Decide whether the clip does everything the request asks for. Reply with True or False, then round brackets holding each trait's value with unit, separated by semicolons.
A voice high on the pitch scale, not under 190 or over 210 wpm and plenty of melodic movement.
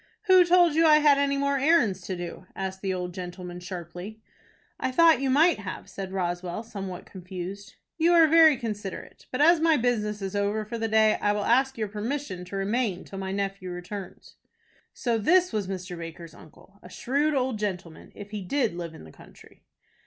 True (210 Hz; 195 wpm; 6.7 semitones)